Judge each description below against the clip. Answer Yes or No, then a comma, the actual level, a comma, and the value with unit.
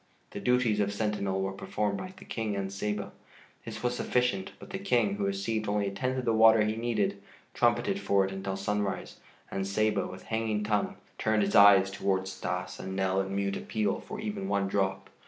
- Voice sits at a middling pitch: No, low, 105 Hz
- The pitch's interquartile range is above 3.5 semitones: No, narrow, 2.4 semitones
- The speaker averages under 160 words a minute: No, average, 200 wpm